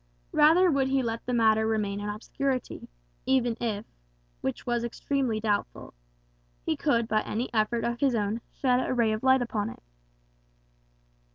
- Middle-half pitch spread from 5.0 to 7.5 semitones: No, average, 3.3 semitones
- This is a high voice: Yes, high, 235 Hz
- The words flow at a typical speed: Yes, average, 160 wpm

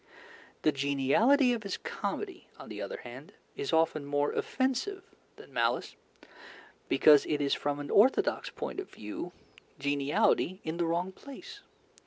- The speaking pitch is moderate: Yes, medium, 170 Hz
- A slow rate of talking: No, average, 145 wpm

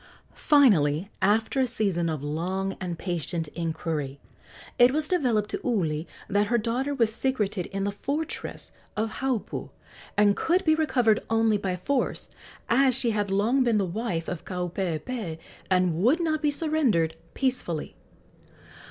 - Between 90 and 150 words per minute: Yes, average, 145 wpm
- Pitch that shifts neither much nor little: No, wide, 6.4 semitones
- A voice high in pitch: Yes, high, 210 Hz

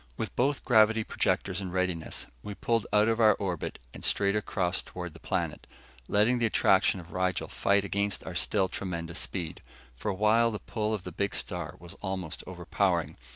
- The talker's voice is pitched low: Yes, low, 100 Hz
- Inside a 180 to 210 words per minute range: Yes, average, 185 wpm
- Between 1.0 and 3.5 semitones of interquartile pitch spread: Yes, average, 3.1 semitones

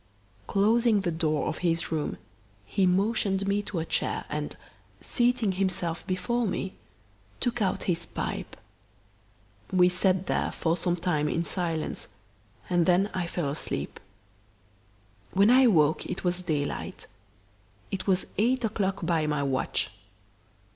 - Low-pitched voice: No, medium, 185 Hz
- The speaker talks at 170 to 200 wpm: No, slow, 135 wpm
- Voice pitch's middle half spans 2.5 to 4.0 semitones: Yes, average, 3.3 semitones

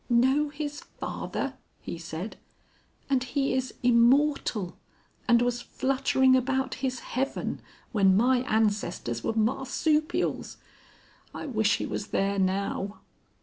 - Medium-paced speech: No, slow, 115 wpm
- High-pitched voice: Yes, high, 245 Hz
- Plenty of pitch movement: No, average, 4.4 semitones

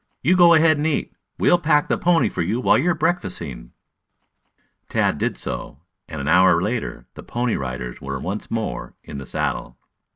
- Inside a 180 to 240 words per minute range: Yes, average, 185 wpm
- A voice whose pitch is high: No, low, 110 Hz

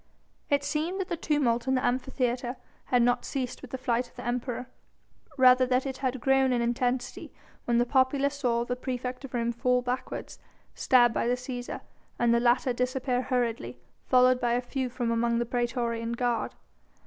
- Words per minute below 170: No, average, 185 wpm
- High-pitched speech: Yes, very high, 250 Hz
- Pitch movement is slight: Yes, narrow, 1.4 semitones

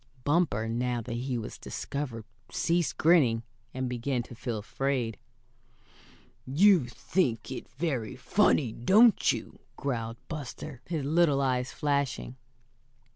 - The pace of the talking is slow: Yes, slow, 120 wpm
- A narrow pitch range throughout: No, average, 4.1 semitones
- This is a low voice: Yes, low, 130 Hz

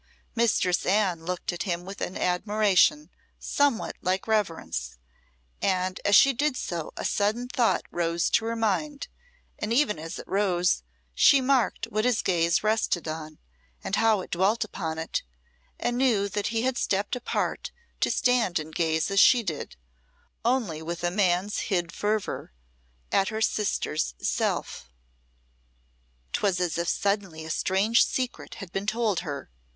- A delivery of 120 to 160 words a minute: Yes, average, 155 wpm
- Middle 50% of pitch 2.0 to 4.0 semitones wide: No, average, 4.6 semitones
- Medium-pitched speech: No, high, 195 Hz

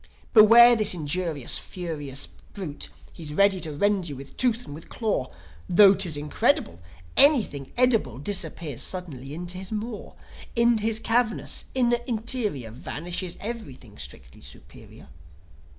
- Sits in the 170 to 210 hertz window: Yes, medium, 185 Hz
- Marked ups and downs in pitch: Yes, wide, 7.4 semitones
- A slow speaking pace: Yes, slow, 130 wpm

